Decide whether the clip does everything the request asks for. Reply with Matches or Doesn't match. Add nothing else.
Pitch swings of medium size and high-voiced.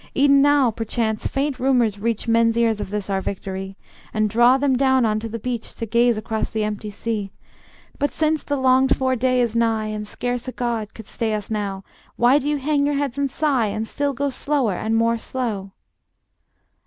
Matches